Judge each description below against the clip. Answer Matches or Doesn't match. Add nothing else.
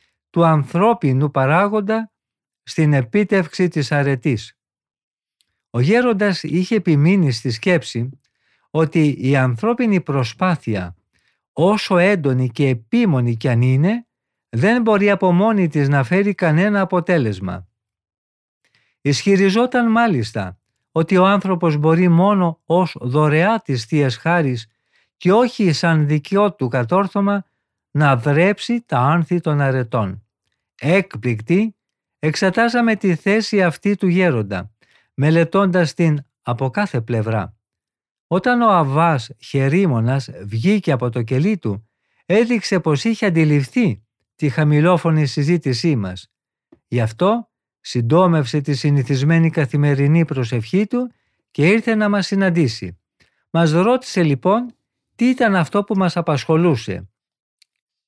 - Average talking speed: Doesn't match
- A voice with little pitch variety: Doesn't match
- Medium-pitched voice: Matches